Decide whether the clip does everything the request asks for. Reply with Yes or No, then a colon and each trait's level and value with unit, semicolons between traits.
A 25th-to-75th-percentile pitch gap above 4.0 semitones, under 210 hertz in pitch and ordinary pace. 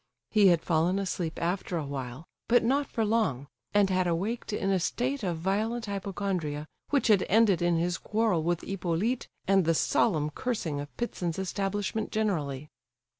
Yes: average, 4.5 semitones; high, 190 Hz; average, 165 wpm